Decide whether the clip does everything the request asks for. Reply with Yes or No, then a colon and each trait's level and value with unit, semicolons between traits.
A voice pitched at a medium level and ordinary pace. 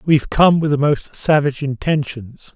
Yes: medium, 145 Hz; average, 165 wpm